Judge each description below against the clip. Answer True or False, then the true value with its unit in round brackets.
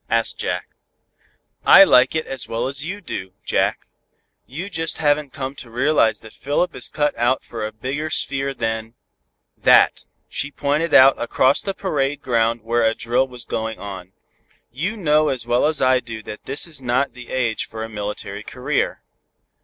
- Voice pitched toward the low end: True (130 Hz)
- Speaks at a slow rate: False (175 wpm)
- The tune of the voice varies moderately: True (4.5 semitones)